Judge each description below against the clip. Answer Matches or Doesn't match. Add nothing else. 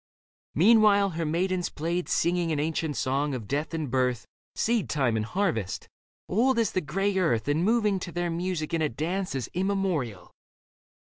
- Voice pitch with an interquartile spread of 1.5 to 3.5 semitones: Doesn't match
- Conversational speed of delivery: Matches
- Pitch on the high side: Doesn't match